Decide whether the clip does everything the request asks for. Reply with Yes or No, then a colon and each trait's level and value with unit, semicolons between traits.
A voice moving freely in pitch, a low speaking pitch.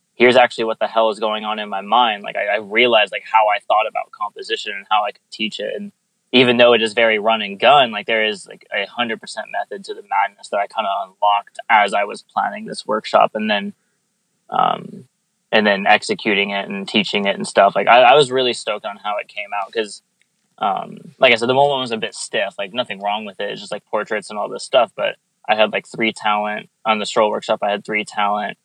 Yes: wide, 6.4 semitones; low, 115 Hz